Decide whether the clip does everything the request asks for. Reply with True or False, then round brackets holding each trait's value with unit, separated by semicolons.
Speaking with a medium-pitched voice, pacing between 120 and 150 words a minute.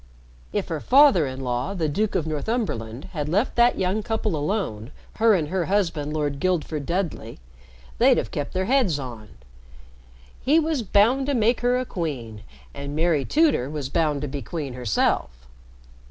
False (160 Hz; 170 wpm)